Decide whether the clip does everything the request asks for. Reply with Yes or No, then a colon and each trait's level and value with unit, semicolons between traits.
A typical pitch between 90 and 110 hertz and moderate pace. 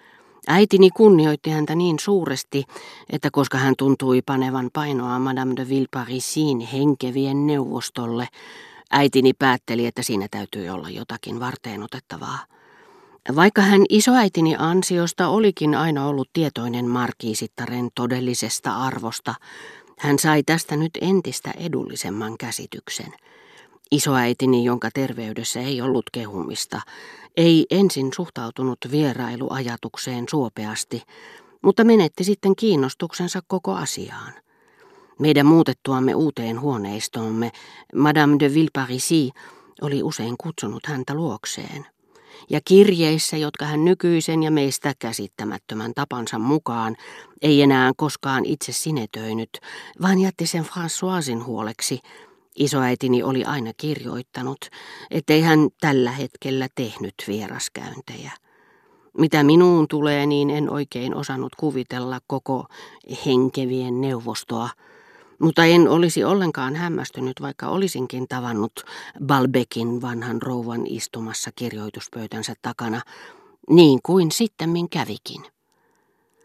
No: low, 135 Hz; average, 105 wpm